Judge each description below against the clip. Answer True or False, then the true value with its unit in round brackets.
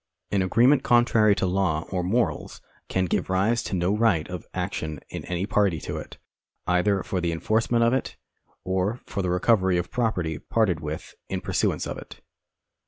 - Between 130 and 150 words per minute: False (175 wpm)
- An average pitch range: True (4.0 semitones)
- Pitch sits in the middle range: False (95 Hz)